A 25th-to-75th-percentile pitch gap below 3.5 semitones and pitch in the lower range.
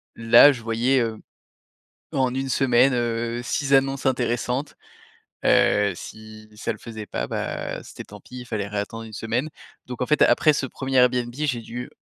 Yes: average, 2.8 semitones; low, 120 Hz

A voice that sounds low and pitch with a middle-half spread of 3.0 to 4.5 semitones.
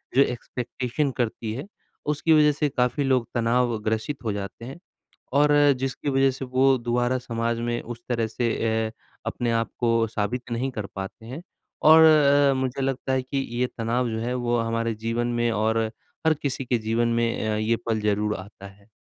No: low, 120 Hz; narrow, 2.6 semitones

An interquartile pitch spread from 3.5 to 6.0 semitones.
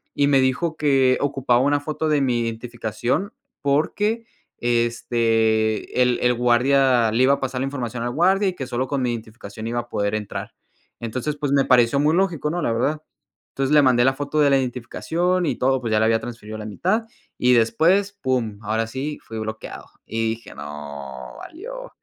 Yes: average, 4.1 semitones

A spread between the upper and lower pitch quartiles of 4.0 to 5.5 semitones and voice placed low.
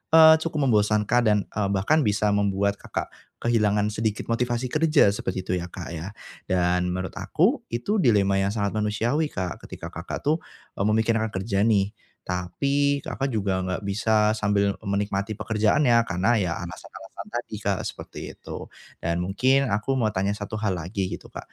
No: average, 3.3 semitones; low, 105 Hz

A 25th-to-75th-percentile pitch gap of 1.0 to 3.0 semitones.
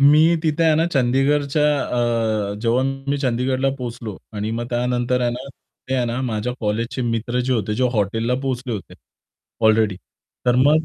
Yes: average, 2.7 semitones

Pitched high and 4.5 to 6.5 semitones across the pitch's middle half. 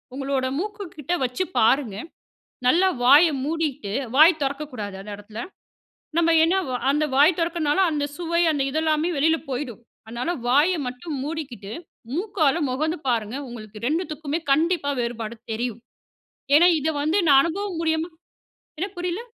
Yes: very high, 295 Hz; average, 4.9 semitones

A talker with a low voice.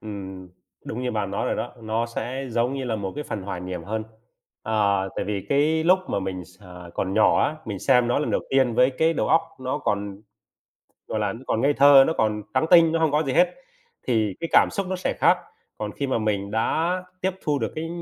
Yes: low, 115 Hz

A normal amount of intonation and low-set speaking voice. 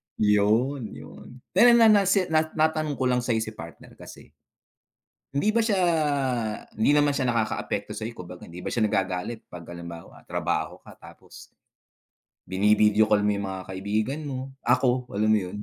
No: wide, 5.7 semitones; low, 115 Hz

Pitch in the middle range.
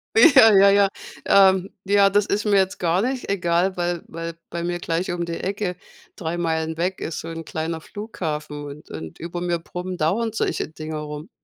Yes: medium, 175 Hz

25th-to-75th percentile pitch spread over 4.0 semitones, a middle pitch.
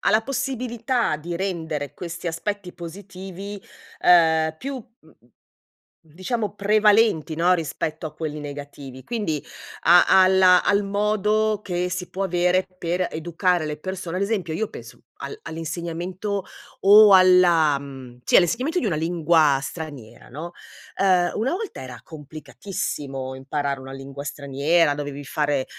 Yes: average, 4.8 semitones; medium, 175 Hz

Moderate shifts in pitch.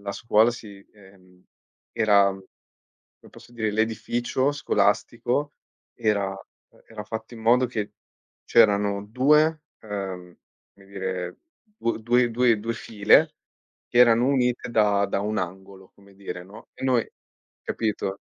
Yes: average, 3.3 semitones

